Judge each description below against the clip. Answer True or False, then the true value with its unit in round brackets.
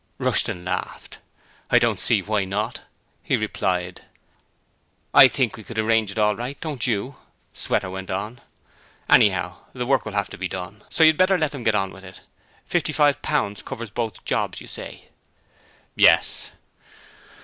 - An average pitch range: True (4.7 semitones)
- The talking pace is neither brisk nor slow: True (160 wpm)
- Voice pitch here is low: True (110 Hz)